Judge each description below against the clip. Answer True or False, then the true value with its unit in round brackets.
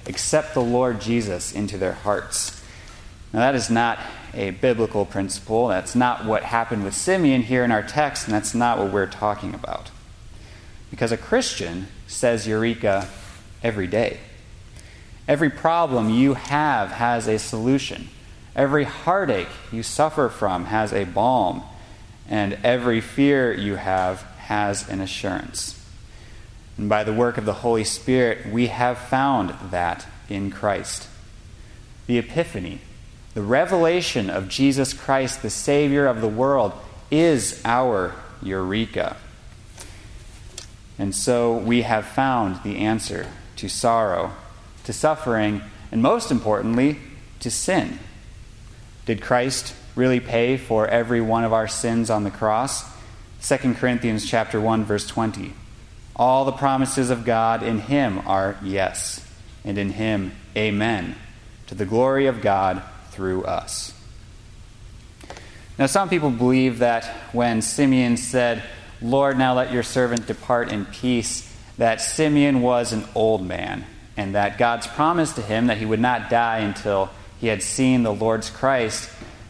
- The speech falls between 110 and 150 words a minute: True (140 wpm)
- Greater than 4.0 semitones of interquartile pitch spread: False (3.3 semitones)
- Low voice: True (110 Hz)